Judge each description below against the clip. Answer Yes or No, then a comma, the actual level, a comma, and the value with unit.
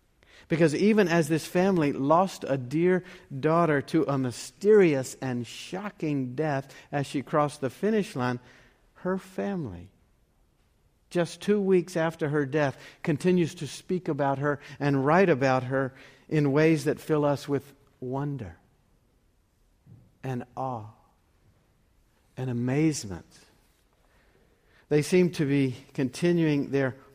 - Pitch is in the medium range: Yes, medium, 145 Hz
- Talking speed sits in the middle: No, slow, 120 wpm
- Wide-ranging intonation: No, average, 4.0 semitones